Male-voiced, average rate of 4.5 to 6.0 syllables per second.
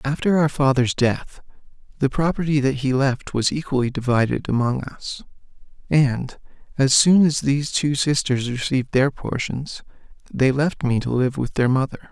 Yes: male; 4.8 syllables/s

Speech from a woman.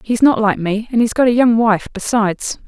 Yes: female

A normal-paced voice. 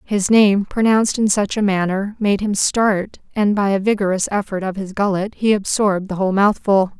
Yes: average, 195 wpm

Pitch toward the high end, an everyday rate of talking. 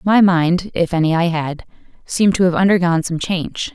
No: medium, 175 Hz; average, 190 wpm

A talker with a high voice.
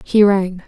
Yes: high, 195 Hz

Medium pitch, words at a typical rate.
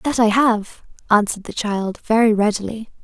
No: high, 215 Hz; average, 160 wpm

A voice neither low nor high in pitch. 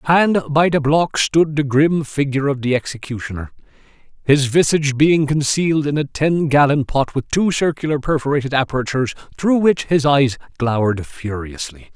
Yes: medium, 145 Hz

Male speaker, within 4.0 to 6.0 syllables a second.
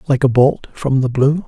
Yes: male; 4.7 syllables/s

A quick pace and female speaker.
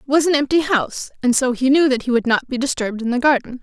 Yes: fast, 300 wpm; female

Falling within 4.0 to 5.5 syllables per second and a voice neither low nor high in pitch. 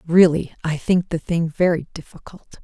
Yes: 4.8 syllables/s; medium, 170 Hz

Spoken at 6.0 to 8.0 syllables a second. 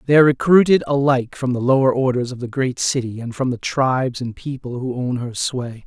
No: 5.6 syllables/s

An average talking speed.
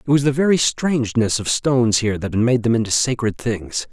No: fast, 230 wpm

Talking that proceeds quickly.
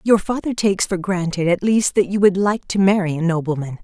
Yes: fast, 235 wpm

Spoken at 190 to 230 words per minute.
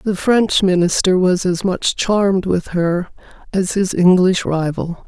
No: average, 155 wpm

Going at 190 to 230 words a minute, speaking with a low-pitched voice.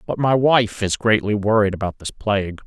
Yes: fast, 205 wpm; low, 105 Hz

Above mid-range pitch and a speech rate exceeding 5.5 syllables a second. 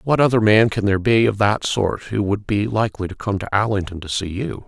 No: low, 105 Hz; 5.8 syllables/s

